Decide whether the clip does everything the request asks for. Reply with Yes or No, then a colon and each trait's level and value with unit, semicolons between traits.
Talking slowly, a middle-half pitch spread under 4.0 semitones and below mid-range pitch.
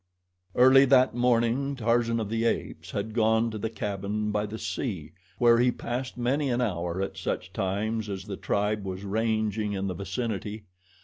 No: average, 175 wpm; average, 2.9 semitones; low, 110 Hz